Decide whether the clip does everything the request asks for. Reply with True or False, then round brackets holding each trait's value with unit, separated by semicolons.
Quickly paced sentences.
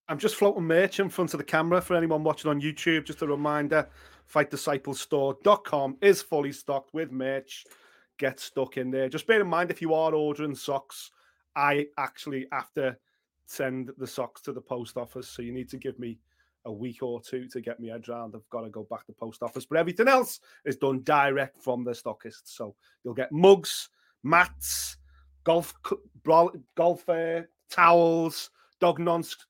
False (180 wpm)